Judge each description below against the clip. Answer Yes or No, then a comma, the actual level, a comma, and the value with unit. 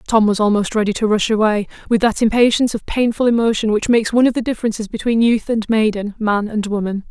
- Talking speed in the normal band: No, fast, 220 wpm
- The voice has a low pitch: No, high, 220 Hz